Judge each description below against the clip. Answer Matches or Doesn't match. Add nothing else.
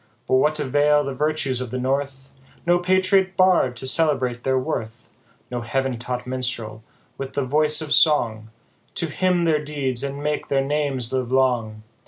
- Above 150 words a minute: Matches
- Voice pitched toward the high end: Doesn't match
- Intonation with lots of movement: Doesn't match